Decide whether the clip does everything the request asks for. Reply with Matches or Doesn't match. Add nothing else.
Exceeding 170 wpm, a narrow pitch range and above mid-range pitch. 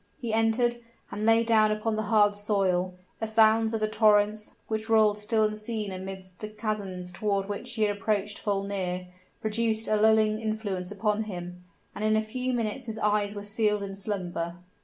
Matches